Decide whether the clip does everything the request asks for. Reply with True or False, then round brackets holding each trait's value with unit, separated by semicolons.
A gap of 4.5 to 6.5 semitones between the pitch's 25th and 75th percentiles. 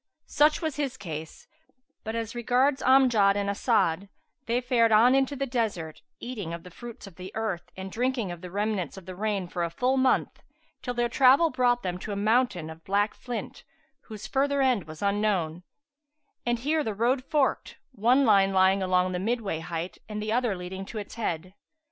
True (5.0 semitones)